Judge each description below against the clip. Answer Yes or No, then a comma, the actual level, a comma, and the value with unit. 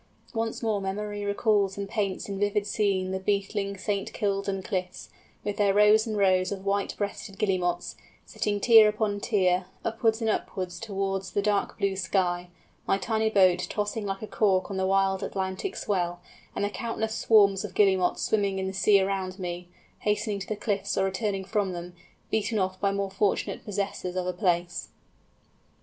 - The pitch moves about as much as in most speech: No, narrow, 1.8 semitones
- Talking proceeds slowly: No, average, 175 wpm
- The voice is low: No, high, 200 Hz